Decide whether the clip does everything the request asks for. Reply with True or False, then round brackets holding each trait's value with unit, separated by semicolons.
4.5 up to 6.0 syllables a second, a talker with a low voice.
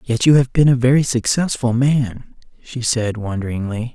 True (4.8 syllables/s; 125 Hz)